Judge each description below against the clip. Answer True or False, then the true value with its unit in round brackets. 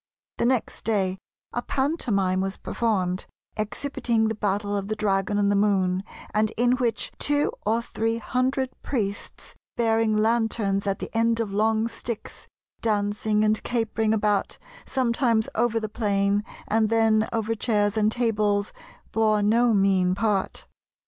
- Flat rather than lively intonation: True (2.1 semitones)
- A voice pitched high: True (215 Hz)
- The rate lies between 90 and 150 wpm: True (140 wpm)